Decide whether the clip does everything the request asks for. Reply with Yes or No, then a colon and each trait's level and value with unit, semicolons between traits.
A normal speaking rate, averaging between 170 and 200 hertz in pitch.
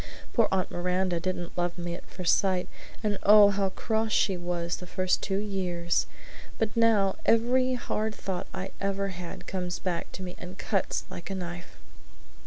Yes: average, 175 wpm; high, 190 Hz